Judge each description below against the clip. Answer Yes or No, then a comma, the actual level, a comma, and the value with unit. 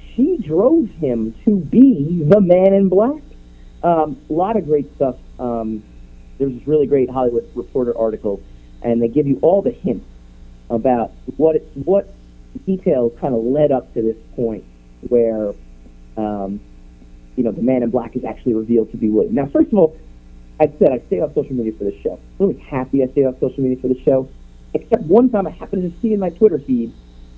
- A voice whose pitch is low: Yes, low, 125 Hz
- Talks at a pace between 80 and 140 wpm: No, average, 200 wpm